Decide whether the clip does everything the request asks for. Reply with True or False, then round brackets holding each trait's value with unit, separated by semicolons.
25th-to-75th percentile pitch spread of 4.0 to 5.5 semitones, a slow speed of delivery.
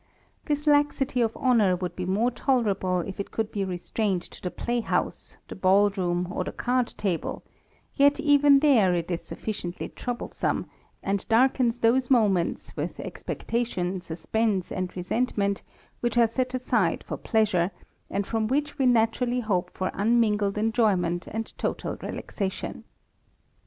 False (4.7 semitones; 145 wpm)